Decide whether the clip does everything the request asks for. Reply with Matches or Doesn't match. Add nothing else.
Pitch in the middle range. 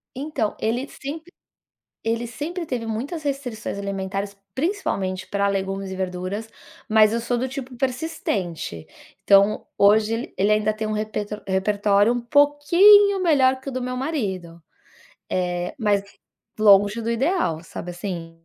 Doesn't match